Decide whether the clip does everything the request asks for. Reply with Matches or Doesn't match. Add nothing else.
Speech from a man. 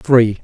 Matches